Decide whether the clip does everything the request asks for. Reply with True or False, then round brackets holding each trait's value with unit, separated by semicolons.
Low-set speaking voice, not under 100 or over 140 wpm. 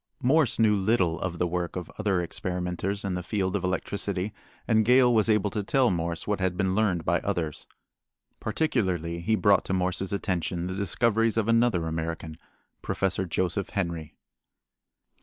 False (95 Hz; 160 wpm)